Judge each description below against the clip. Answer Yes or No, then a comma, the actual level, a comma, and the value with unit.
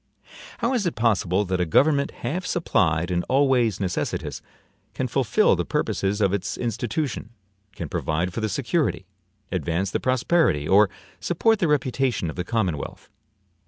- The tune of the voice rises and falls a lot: Yes, wide, 7.5 semitones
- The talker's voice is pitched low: Yes, low, 110 Hz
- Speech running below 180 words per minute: Yes, average, 150 wpm